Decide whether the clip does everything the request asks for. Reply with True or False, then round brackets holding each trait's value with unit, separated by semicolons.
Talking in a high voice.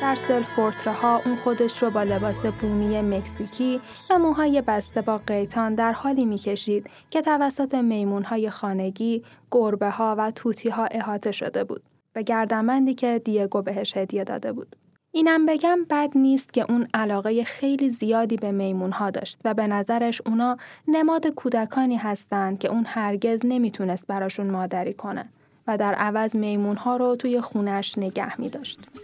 True (225 Hz)